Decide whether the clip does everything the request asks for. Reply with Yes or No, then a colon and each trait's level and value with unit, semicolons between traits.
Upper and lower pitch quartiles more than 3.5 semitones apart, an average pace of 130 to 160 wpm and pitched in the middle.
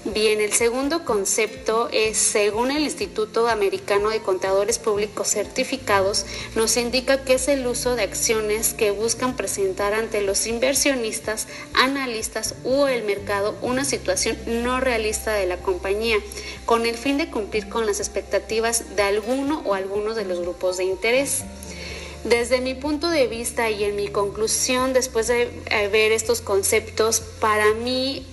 No: average, 3.9 semitones; average, 150 wpm; high, 225 Hz